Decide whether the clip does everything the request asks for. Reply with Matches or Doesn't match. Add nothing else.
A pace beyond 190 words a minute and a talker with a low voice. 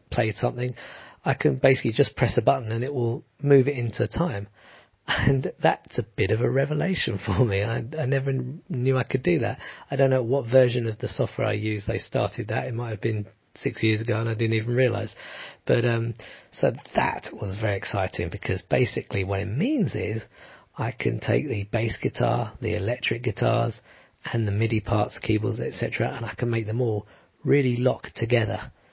Matches